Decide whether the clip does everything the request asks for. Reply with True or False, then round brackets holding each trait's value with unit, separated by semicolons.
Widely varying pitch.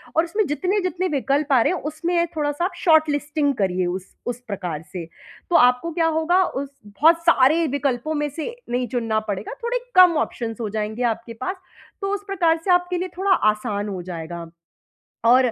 True (7.4 semitones)